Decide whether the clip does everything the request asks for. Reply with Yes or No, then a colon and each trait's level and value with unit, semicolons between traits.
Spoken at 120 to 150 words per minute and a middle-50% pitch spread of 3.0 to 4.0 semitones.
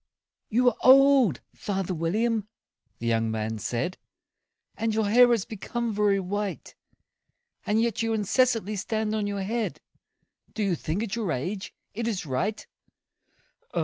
Yes: average, 145 wpm; average, 3.6 semitones